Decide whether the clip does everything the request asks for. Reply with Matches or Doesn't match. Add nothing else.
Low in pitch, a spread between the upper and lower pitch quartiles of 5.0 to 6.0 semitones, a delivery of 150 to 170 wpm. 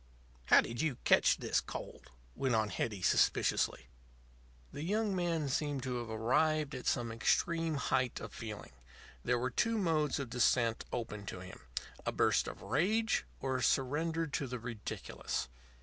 Matches